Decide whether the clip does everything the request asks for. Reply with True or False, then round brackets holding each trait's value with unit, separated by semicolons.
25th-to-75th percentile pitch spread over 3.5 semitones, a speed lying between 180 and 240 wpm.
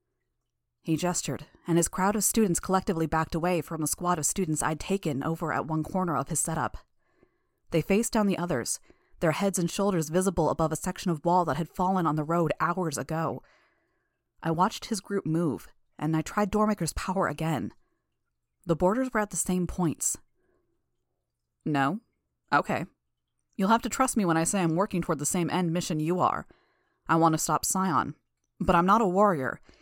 False (3.1 semitones; 190 wpm)